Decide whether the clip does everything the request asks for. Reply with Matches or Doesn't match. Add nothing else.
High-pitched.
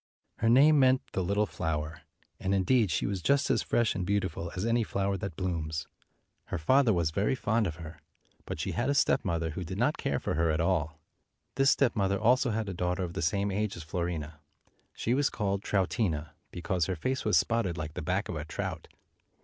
Doesn't match